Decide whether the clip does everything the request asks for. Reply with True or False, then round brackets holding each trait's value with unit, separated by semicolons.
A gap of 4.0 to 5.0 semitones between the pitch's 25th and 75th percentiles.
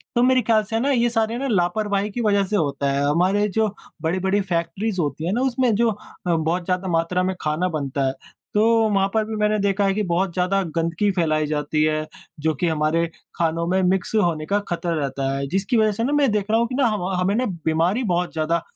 True (4.4 semitones)